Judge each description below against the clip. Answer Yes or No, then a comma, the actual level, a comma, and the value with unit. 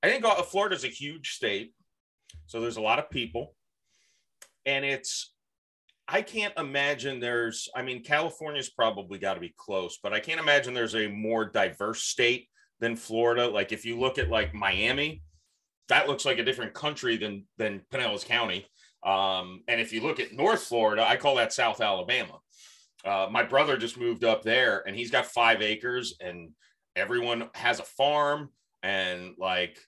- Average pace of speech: Yes, average, 175 wpm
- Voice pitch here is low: Yes, low, 115 Hz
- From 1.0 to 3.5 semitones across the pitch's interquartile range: No, average, 4.4 semitones